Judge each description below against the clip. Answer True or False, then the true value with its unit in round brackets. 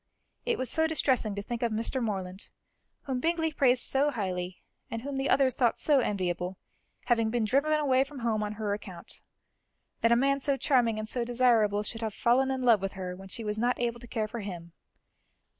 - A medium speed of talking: False (210 wpm)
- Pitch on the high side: True (235 Hz)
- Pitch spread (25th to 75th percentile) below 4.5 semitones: True (4.1 semitones)